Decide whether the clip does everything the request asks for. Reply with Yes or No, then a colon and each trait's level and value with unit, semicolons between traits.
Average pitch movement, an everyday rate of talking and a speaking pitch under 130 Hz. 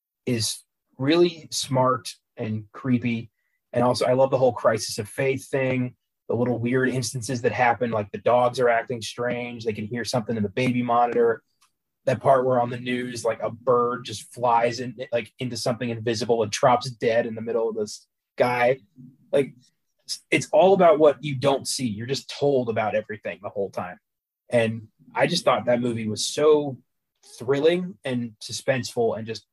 No: narrow, 2.0 semitones; average, 180 wpm; low, 120 Hz